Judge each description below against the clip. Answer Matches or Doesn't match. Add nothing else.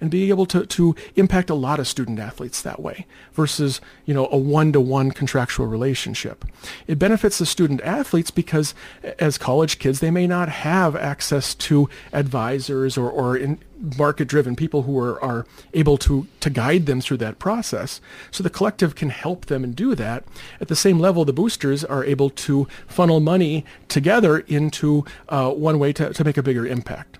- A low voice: Doesn't match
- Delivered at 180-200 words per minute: Matches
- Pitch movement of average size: Matches